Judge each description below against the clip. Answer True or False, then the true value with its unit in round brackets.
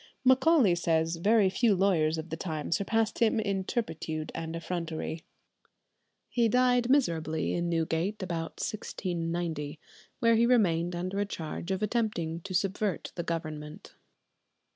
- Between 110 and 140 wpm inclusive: True (135 wpm)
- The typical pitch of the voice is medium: True (175 Hz)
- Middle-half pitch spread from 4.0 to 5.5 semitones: True (4.8 semitones)